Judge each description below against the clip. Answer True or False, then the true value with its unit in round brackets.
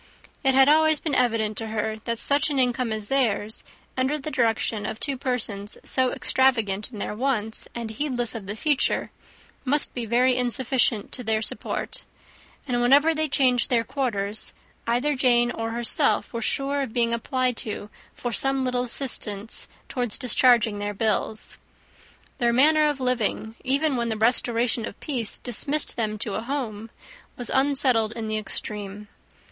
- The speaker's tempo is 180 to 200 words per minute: False (165 wpm)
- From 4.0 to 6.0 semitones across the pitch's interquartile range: False (3.4 semitones)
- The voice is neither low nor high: False (240 Hz)